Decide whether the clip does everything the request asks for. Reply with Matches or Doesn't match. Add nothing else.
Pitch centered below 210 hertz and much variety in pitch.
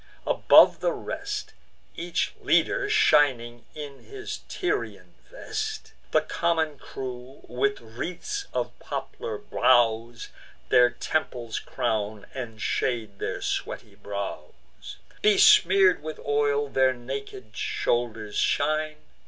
Matches